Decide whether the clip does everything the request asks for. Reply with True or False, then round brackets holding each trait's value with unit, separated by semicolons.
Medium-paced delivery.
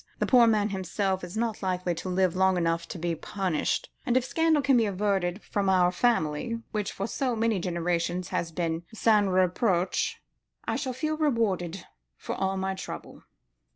True (175 wpm)